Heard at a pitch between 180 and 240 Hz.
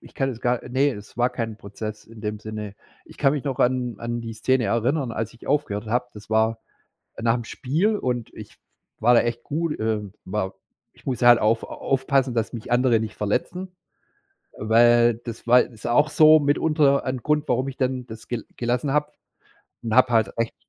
No: low, 120 Hz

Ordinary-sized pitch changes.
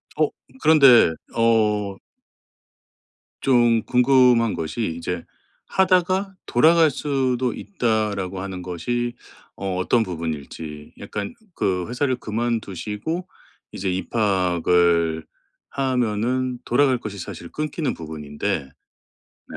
No: wide, 6.0 semitones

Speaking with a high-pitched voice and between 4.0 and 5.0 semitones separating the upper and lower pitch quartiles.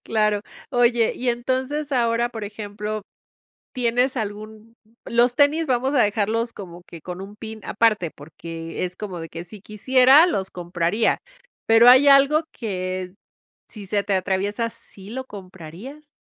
Yes: high, 215 Hz; average, 4.4 semitones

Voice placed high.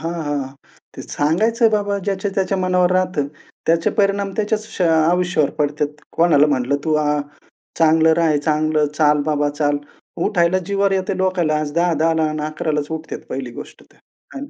No: medium, 165 Hz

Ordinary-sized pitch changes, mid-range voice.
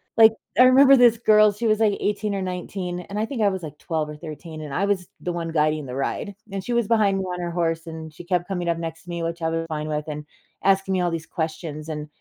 Yes: average, 4.0 semitones; medium, 175 Hz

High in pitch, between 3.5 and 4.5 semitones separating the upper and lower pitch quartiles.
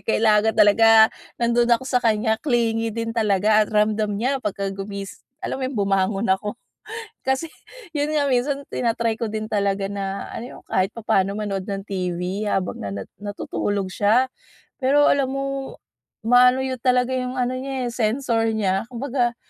Yes: high, 225 Hz; average, 3.8 semitones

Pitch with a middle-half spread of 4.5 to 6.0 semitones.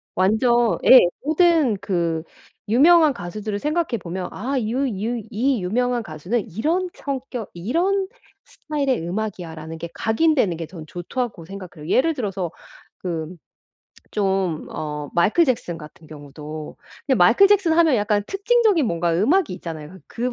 No: wide, 8.0 semitones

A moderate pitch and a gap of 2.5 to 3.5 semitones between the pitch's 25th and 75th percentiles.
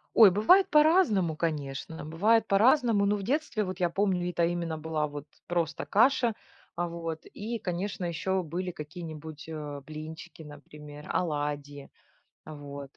No: medium, 170 Hz; average, 4.8 semitones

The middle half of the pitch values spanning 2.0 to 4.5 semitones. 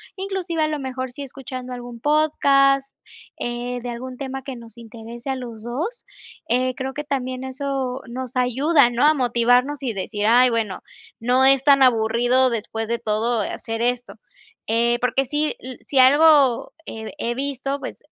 Yes: narrow, 2.5 semitones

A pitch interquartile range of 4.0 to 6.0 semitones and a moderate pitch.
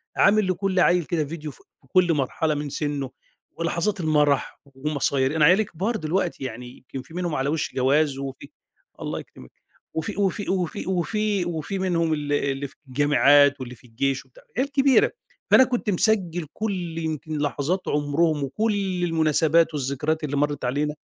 Yes: average, 4.3 semitones; medium, 155 Hz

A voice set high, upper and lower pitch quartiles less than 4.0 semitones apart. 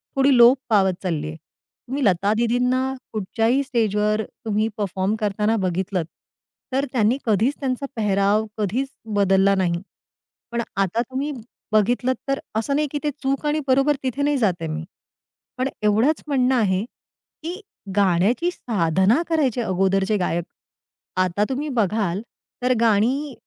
No: high, 220 Hz; average, 5.2 semitones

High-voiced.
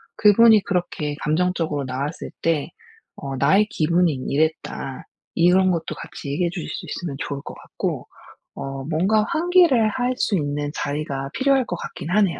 No: medium, 170 Hz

